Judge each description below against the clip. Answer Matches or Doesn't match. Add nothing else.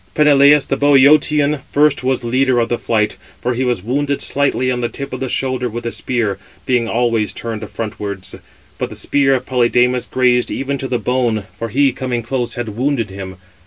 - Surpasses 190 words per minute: Matches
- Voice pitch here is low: Matches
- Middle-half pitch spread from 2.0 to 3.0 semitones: Matches